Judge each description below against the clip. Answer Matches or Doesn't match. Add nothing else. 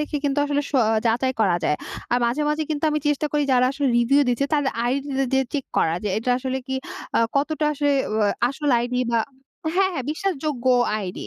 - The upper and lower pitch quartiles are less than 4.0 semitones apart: Matches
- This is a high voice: Matches